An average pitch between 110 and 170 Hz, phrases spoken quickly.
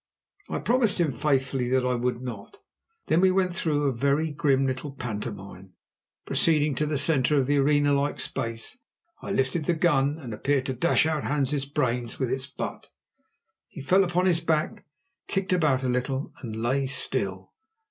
No: medium, 140 Hz; average, 175 wpm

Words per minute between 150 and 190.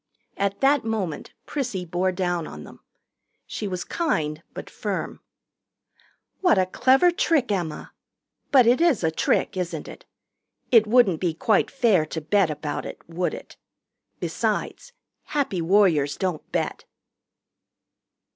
No: slow, 135 wpm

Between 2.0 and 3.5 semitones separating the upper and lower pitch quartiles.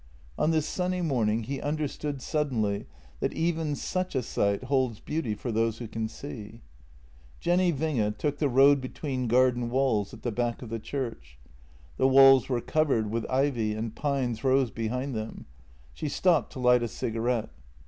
No: average, 4.1 semitones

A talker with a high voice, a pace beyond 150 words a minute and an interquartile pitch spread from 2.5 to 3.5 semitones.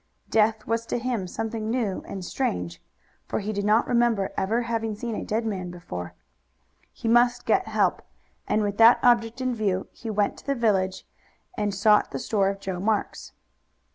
Yes: high, 215 Hz; average, 180 wpm; average, 2.8 semitones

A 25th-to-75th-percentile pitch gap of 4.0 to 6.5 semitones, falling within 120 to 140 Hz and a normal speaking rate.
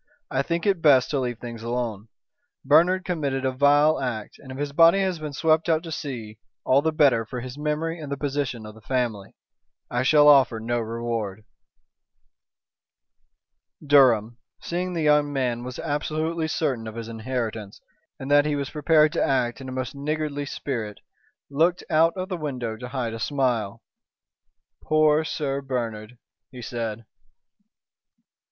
Yes: average, 4.4 semitones; low, 135 Hz; average, 165 wpm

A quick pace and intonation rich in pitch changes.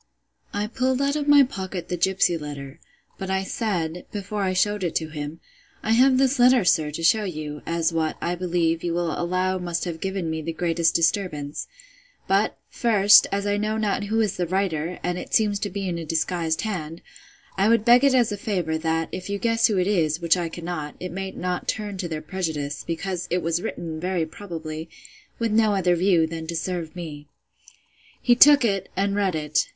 No: fast, 210 wpm; average, 3.8 semitones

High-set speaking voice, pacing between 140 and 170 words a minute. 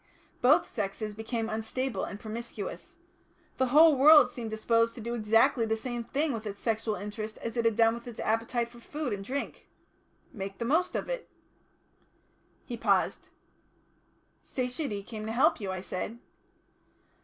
Yes: high, 230 Hz; average, 160 wpm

